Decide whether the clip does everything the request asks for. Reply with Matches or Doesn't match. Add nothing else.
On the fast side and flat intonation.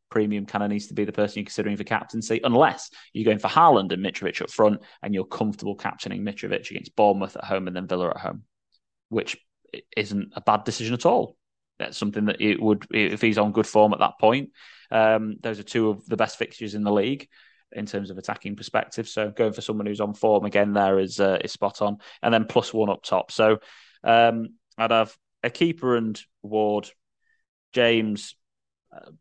Matches